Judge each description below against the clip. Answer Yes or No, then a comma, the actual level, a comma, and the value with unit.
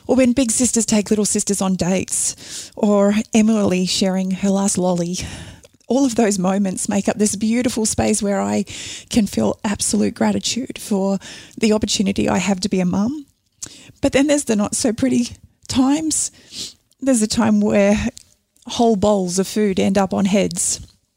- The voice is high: Yes, high, 210 Hz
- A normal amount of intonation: Yes, average, 3.4 semitones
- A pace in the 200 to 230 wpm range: No, average, 165 wpm